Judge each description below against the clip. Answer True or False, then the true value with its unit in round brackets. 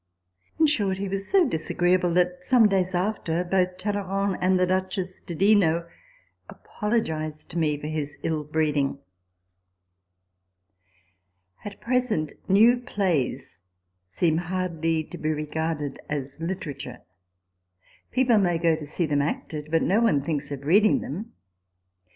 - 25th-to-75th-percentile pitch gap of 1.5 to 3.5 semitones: False (4.5 semitones)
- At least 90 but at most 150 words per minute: True (140 wpm)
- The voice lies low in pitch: False (170 Hz)